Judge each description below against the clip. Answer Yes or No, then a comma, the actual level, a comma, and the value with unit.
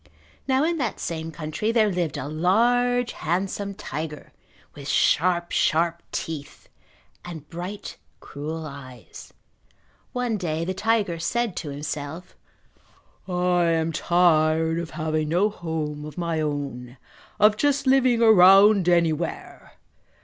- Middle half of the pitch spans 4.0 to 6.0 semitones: Yes, average, 4.8 semitones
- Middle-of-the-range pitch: Yes, medium, 170 Hz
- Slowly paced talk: Yes, slow, 120 wpm